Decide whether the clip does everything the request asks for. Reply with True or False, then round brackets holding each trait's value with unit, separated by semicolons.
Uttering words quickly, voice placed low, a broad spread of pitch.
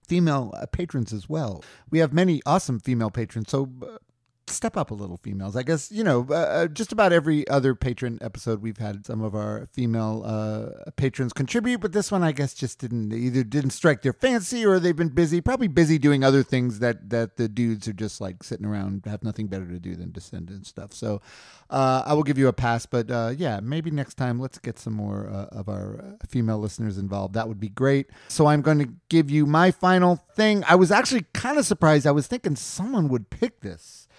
True (220 wpm; 130 Hz; 6.8 semitones)